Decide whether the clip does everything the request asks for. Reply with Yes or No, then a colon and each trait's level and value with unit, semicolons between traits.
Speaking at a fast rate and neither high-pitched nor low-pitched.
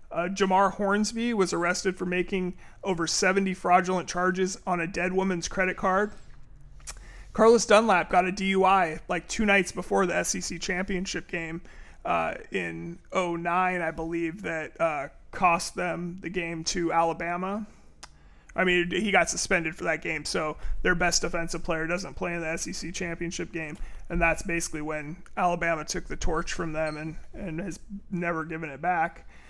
No: average, 165 wpm; medium, 175 Hz